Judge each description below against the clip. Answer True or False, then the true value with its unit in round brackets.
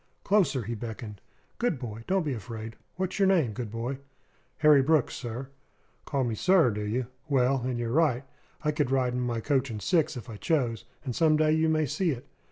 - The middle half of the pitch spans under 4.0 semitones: False (5.0 semitones)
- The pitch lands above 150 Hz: False (130 Hz)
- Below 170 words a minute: False (205 wpm)